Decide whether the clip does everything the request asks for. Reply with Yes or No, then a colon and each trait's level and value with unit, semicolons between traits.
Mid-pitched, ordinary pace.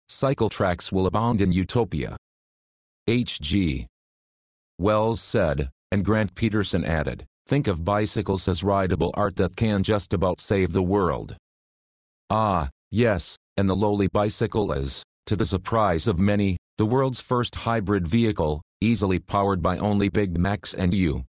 No: low, 100 Hz; average, 145 wpm